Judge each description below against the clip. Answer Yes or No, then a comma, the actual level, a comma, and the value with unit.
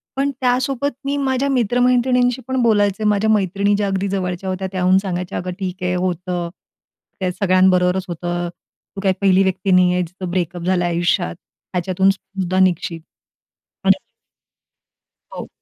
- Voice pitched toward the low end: No, high, 190 Hz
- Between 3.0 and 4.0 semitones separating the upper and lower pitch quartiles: No, narrow, 2.6 semitones